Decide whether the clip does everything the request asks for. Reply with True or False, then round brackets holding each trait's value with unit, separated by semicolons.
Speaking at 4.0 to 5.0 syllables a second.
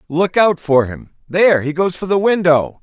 True (4.7 syllables/s)